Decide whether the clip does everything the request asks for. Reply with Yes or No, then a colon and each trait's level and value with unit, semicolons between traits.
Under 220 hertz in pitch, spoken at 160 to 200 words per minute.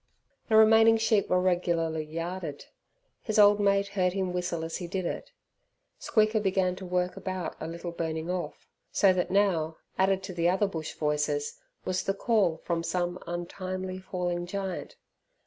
Yes: medium, 185 Hz; average, 165 wpm